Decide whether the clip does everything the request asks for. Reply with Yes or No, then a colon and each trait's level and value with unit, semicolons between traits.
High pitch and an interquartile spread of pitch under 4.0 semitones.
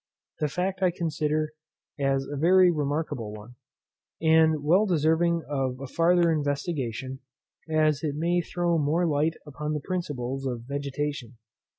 No: medium, 150 Hz; average, 3.3 semitones